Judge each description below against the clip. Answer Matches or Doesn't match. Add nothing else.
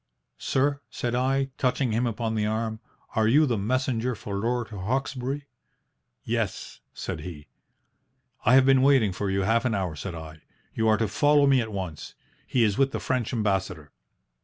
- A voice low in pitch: Matches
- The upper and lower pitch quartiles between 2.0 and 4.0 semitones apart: Doesn't match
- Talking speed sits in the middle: Matches